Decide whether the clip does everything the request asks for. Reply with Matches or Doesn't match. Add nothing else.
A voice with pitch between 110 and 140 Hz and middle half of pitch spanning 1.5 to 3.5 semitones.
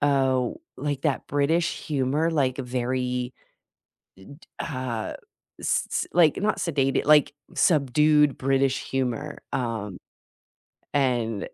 Matches